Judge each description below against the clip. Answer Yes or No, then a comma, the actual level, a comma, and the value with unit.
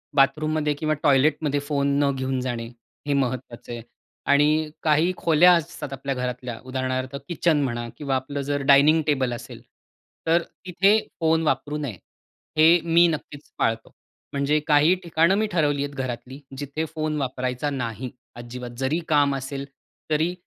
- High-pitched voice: No, medium, 145 Hz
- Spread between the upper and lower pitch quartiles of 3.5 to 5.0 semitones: No, average, 3.1 semitones